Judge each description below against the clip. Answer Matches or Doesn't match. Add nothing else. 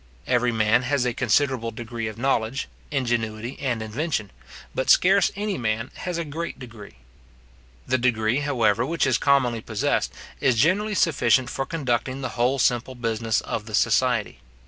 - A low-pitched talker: Matches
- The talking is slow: Doesn't match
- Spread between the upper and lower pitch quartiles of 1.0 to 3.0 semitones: Doesn't match